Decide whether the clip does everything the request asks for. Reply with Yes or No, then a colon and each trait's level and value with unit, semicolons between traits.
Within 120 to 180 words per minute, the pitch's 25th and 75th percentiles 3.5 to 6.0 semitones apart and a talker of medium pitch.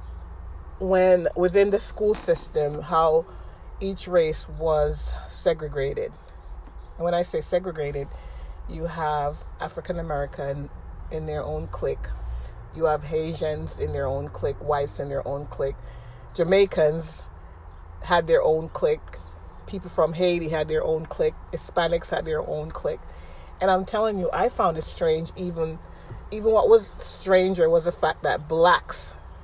Yes: average, 145 wpm; wide, 5.5 semitones; medium, 160 Hz